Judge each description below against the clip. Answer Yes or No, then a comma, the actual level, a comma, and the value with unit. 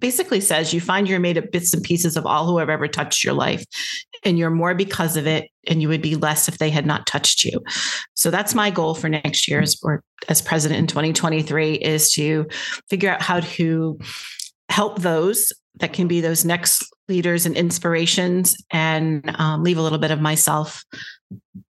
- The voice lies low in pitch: No, medium, 165 Hz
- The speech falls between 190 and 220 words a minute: Yes, average, 200 wpm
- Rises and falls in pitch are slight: Yes, narrow, 2.3 semitones